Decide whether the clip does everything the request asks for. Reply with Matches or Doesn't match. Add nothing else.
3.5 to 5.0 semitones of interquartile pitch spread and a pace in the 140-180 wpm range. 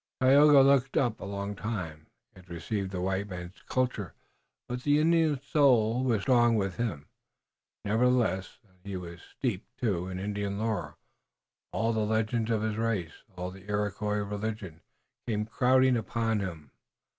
Matches